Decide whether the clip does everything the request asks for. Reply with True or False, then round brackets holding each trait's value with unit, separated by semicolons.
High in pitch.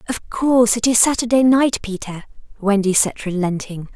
True (220 Hz)